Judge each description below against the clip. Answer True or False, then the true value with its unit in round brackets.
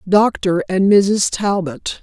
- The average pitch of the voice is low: False (190 Hz)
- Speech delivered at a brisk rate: False (120 wpm)